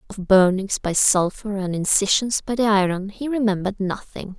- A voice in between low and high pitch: No, high, 200 Hz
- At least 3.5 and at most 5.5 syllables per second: Yes, 5.0 syllables/s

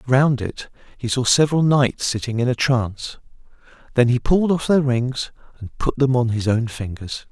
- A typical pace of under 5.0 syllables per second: No, 5.2 syllables/s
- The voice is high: No, low, 125 Hz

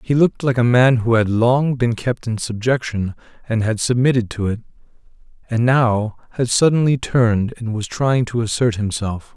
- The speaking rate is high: No, average, 180 wpm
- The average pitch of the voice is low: Yes, low, 115 Hz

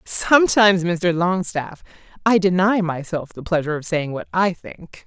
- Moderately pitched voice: Yes, medium, 180 Hz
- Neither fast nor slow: Yes, average, 155 wpm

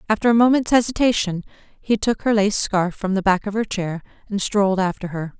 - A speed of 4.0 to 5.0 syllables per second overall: No, 5.5 syllables/s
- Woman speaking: Yes, female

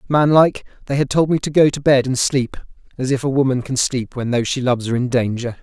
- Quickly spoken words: Yes, fast, 255 wpm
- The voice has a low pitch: Yes, low, 130 Hz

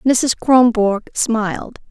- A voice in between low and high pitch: No, high, 230 Hz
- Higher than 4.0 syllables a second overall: No, 3.1 syllables/s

